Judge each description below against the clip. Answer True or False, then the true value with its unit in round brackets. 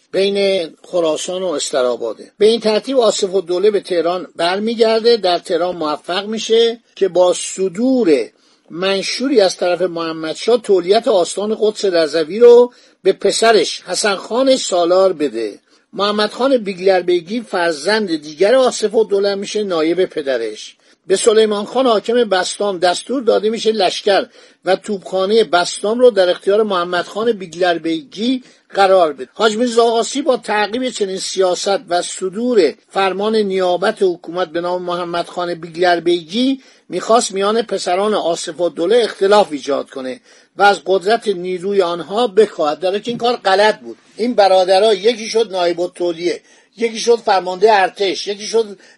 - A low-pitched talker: False (195 Hz)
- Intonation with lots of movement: False (4.2 semitones)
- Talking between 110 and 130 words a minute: False (145 wpm)